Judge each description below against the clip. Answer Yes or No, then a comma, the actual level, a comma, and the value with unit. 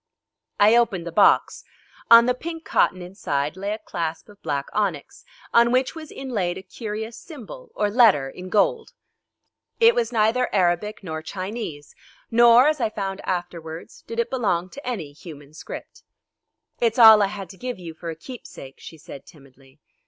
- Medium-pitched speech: No, high, 205 Hz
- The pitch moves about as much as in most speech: No, wide, 6.0 semitones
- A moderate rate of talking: Yes, average, 170 wpm